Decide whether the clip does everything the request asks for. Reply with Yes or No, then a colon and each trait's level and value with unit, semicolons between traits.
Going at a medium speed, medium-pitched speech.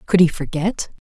Yes: average, 175 wpm; medium, 175 Hz